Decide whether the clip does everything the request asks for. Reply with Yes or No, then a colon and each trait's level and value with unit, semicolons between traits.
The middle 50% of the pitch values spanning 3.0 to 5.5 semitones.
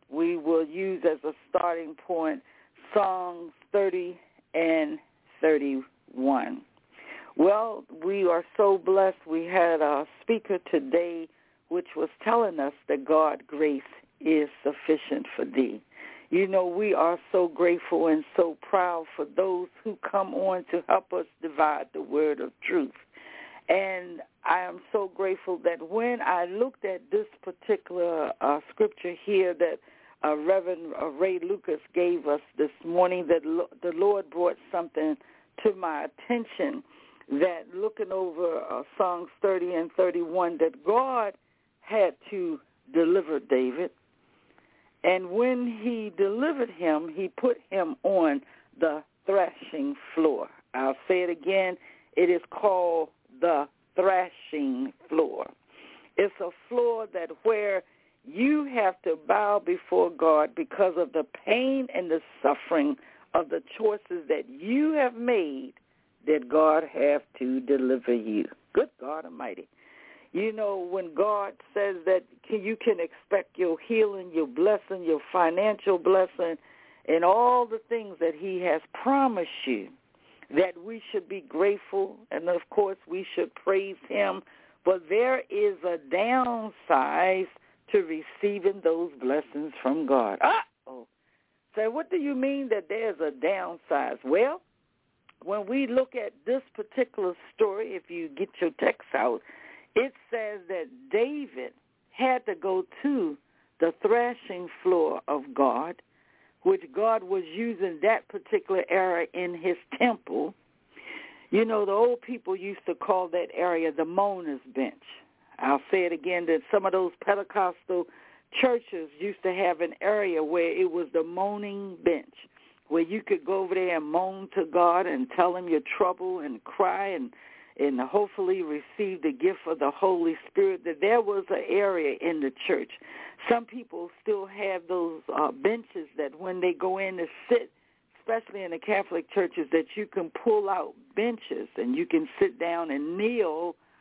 No: wide, 6.8 semitones